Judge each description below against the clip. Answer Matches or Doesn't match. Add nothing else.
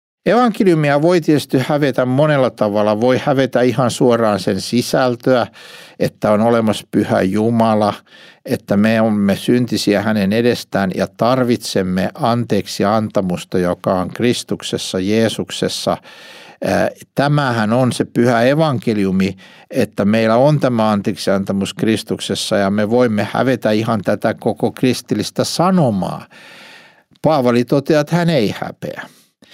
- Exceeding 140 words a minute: Doesn't match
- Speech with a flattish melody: Doesn't match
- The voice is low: Matches